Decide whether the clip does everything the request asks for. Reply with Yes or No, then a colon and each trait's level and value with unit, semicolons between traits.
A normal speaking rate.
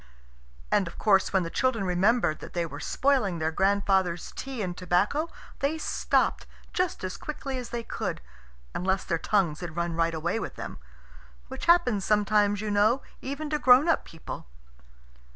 Yes: average, 170 wpm